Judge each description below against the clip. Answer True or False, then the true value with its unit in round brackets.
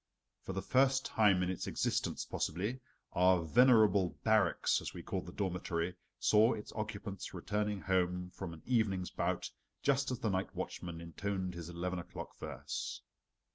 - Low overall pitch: True (95 Hz)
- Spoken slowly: False (155 wpm)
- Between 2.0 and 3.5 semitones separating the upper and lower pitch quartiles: True (3.2 semitones)